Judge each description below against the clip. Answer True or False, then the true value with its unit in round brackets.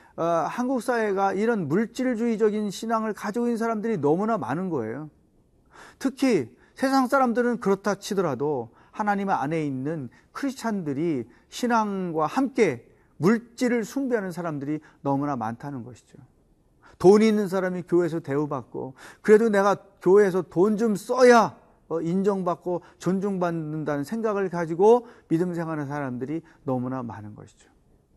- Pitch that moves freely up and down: True (6.6 semitones)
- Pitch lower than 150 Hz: False (190 Hz)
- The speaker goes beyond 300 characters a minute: True (315 characters per minute)